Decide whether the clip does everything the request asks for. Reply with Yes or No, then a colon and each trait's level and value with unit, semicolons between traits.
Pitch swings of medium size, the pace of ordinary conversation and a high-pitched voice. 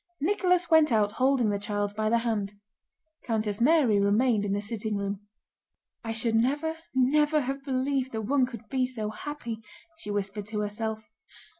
Yes: average, 4.5 semitones; average, 165 wpm; high, 230 Hz